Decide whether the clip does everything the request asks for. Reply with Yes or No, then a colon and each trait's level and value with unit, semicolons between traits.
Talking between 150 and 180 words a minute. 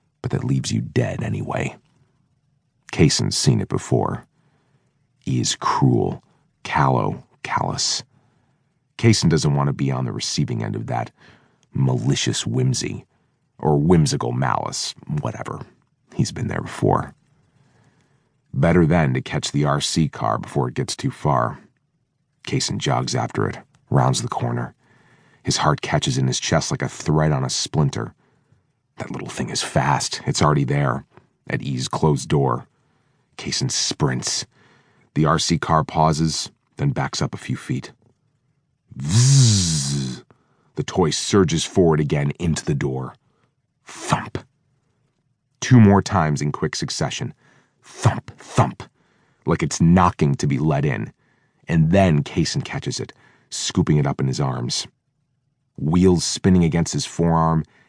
No: slow, 135 wpm